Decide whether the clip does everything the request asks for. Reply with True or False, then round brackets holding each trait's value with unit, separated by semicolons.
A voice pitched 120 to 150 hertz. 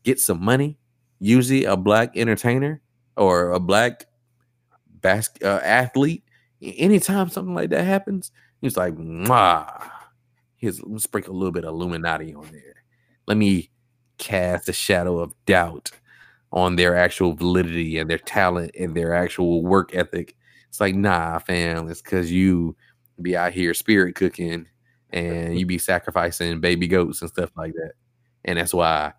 False (95 Hz)